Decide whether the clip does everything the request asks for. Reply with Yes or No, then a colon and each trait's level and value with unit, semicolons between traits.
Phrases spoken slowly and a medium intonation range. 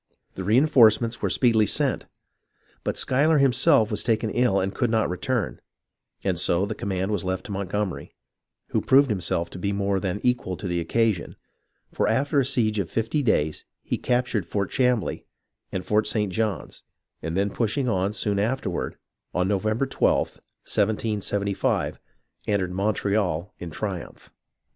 No: average, 160 wpm; average, 3.6 semitones